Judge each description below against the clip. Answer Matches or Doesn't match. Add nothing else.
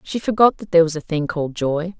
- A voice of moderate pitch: Matches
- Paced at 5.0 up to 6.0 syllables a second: Doesn't match